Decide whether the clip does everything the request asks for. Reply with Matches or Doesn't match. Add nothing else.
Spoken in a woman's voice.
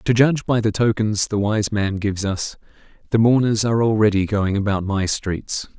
Doesn't match